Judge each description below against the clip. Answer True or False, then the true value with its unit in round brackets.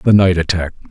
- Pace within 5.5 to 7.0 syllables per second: True (5.6 syllables/s)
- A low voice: True (90 Hz)